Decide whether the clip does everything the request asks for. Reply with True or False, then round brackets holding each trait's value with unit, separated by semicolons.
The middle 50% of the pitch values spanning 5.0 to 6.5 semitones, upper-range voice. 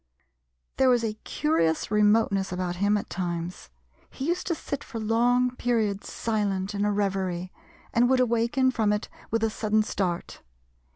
False (3.6 semitones; 210 Hz)